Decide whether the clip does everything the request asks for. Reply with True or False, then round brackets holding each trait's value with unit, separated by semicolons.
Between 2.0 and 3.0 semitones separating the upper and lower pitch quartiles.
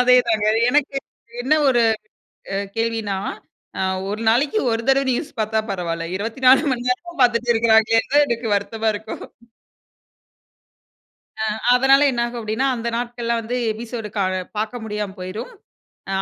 True (2.5 semitones)